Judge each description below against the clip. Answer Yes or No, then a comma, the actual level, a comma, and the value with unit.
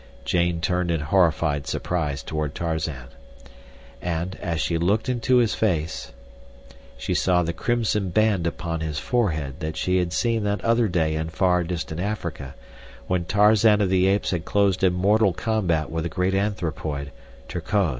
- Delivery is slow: No, average, 155 wpm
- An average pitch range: Yes, average, 4.2 semitones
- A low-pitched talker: Yes, very low, 90 Hz